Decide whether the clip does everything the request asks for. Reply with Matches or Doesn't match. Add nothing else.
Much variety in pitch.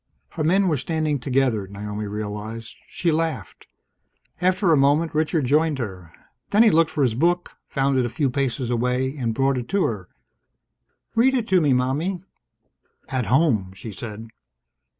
Matches